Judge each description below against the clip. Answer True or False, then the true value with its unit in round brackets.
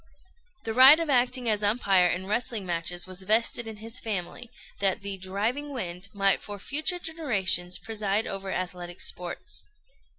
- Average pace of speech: True (155 wpm)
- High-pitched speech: True (205 Hz)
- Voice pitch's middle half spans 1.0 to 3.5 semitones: False (4.3 semitones)